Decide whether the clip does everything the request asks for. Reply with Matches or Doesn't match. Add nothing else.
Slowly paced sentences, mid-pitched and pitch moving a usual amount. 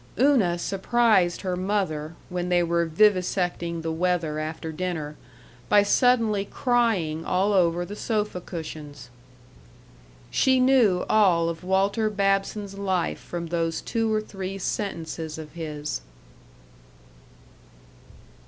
Matches